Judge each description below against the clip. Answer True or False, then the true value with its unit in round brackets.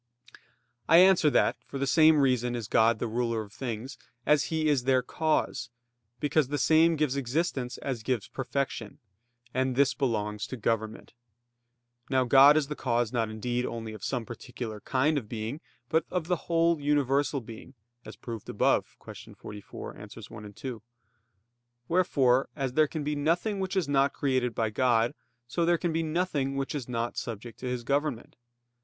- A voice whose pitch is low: True (130 Hz)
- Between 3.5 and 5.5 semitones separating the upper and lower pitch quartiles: True (4.3 semitones)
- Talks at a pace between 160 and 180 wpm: True (175 wpm)